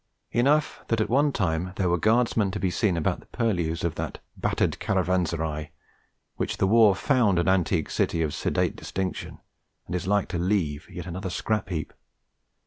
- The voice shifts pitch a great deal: No, average, 4.2 semitones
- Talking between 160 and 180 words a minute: Yes, average, 175 wpm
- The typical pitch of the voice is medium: No, very low, 95 Hz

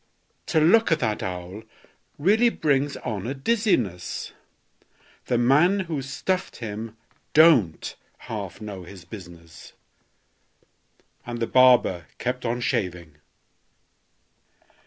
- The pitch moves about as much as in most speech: No, wide, 8.3 semitones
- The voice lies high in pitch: No, low, 120 Hz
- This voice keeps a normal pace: No, slow, 105 wpm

